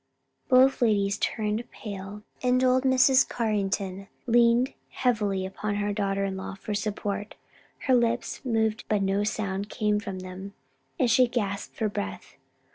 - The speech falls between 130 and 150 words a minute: Yes, average, 145 wpm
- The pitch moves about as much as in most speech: Yes, average, 3.3 semitones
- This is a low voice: No, high, 210 Hz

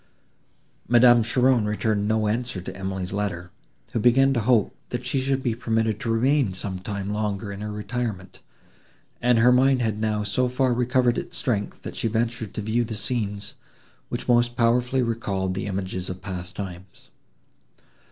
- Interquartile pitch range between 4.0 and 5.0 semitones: No, average, 3.5 semitones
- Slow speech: No, average, 170 wpm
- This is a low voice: Yes, low, 110 Hz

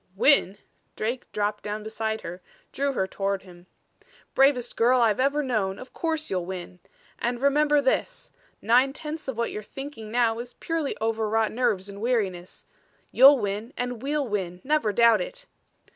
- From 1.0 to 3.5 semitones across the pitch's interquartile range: No, average, 4.8 semitones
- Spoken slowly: No, average, 160 wpm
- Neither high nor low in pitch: No, high, 235 Hz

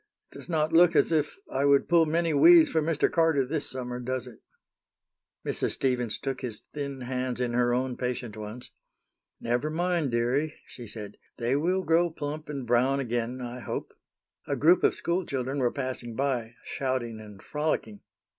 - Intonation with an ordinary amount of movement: Yes, average, 4.2 semitones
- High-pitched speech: No, low, 130 Hz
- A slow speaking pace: No, average, 175 wpm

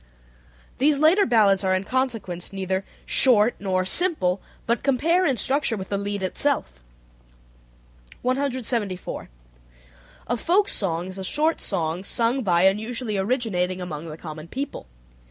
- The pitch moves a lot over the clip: Yes, wide, 5.8 semitones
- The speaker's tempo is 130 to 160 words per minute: Yes, slow, 135 wpm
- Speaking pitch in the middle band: No, high, 205 Hz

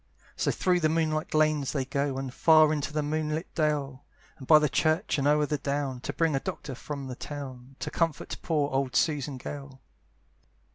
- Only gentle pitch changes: Yes, narrow, 2.2 semitones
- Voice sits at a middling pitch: Yes, medium, 145 Hz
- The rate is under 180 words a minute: No, average, 190 wpm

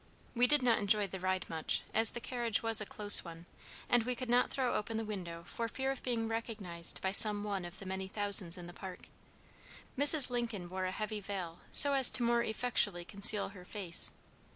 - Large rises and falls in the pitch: No, average, 4.1 semitones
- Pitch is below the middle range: No, high, 210 Hz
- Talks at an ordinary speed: No, fast, 210 wpm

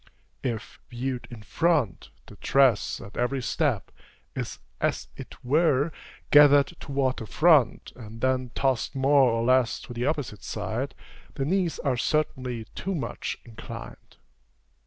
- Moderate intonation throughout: Yes, average, 3.5 semitones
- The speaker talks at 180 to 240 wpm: No, slow, 135 wpm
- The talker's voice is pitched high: No, low, 130 Hz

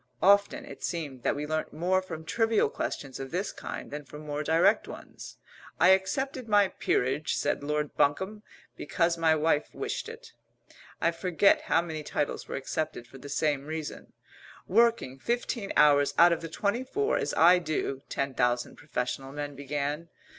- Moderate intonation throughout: Yes, average, 4.8 semitones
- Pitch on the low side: No, medium, 160 Hz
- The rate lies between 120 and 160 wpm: No, average, 170 wpm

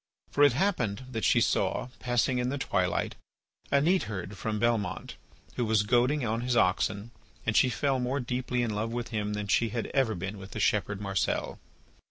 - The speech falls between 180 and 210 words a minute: Yes, average, 190 wpm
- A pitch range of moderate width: Yes, average, 3.4 semitones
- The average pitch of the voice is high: No, low, 115 Hz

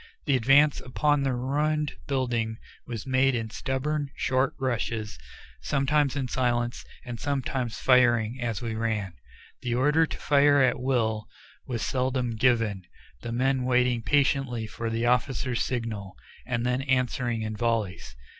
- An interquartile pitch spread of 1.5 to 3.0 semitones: Yes, average, 2.7 semitones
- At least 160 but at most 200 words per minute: No, average, 140 wpm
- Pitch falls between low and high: No, low, 125 Hz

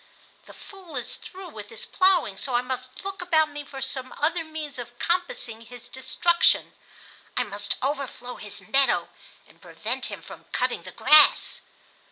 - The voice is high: Yes, very high, 275 Hz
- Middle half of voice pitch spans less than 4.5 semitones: No, wide, 5.5 semitones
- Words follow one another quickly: No, average, 165 wpm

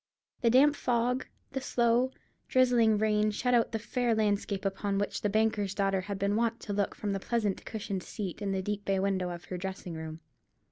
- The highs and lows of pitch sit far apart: No, average, 3.1 semitones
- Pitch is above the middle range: Yes, high, 205 Hz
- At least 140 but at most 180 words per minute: No, average, 200 wpm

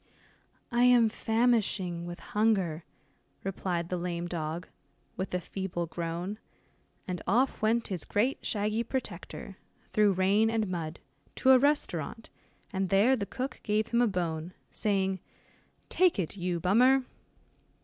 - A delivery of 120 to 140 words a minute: Yes, slow, 135 wpm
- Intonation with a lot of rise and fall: No, average, 4.4 semitones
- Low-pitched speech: No, high, 195 Hz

